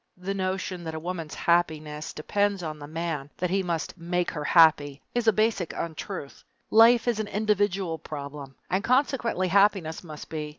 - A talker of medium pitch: Yes, medium, 175 Hz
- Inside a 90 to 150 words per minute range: No, average, 170 wpm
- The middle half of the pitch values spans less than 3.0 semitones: No, average, 4.5 semitones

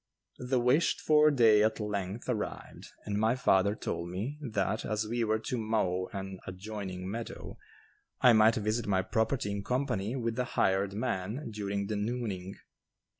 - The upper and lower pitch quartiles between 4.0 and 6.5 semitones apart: No, average, 3.3 semitones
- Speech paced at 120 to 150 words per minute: No, average, 160 wpm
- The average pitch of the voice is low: Yes, low, 110 Hz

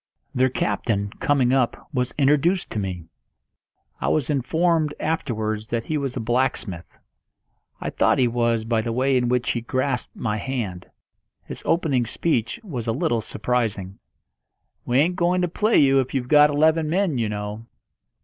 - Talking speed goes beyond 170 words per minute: No, average, 165 wpm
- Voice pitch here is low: Yes, low, 125 Hz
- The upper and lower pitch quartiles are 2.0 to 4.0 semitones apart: No, average, 4.5 semitones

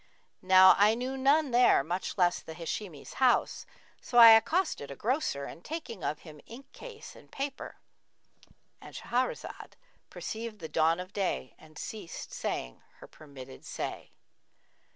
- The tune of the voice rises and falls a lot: Yes, wide, 8.0 semitones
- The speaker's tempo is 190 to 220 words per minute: No, average, 145 wpm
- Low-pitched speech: No, high, 205 Hz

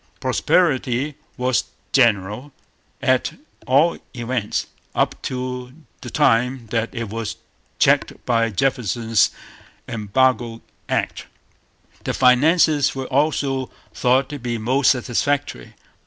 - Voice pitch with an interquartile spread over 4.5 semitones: No, narrow, 2.6 semitones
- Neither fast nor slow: No, slow, 100 wpm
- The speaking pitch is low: Yes, low, 125 Hz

